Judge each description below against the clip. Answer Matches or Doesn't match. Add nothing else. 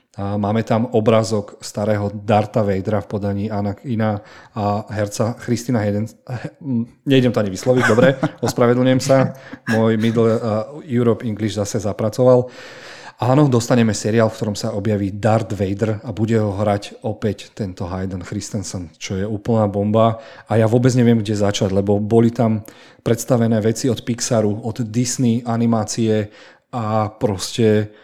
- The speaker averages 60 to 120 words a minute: Doesn't match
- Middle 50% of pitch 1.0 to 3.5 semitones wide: Matches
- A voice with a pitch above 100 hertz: Matches